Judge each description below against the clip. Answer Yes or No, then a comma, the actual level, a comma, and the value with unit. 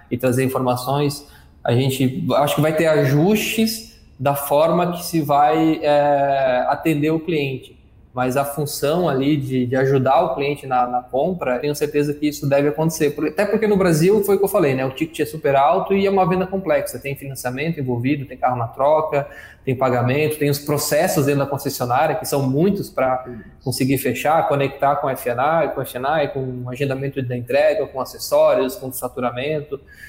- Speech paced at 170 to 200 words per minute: Yes, fast, 185 wpm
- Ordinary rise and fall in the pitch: Yes, average, 3.2 semitones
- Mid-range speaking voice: Yes, medium, 145 Hz